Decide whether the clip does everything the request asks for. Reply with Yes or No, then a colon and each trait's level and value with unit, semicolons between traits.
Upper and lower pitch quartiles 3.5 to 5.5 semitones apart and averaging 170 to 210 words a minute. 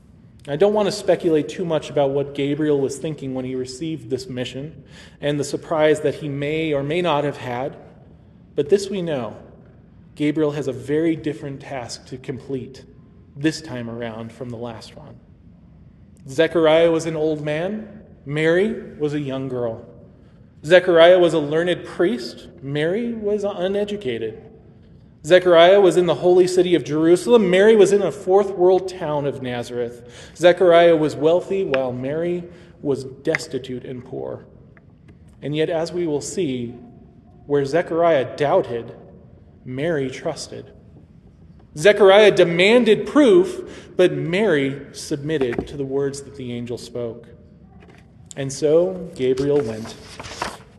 No: average, 4.9 semitones; average, 140 wpm